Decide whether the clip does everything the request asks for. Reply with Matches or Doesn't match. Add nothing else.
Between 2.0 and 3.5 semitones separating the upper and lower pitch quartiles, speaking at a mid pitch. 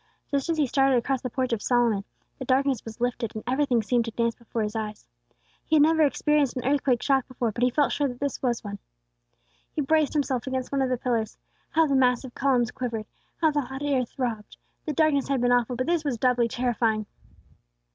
Doesn't match